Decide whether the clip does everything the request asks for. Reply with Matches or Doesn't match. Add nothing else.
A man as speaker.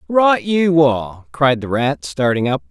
Matches